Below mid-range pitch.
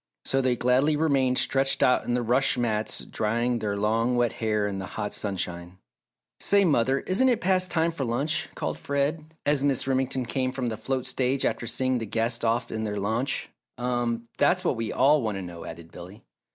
Yes: low, 125 Hz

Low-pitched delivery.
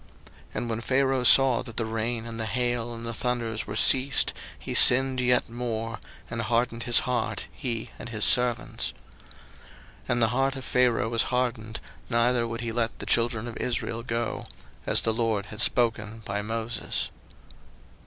Yes: low, 115 Hz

